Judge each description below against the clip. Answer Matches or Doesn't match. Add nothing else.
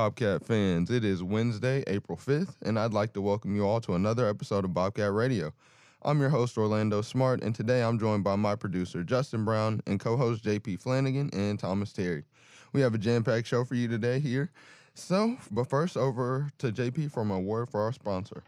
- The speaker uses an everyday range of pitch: Matches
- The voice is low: Matches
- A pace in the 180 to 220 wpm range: Matches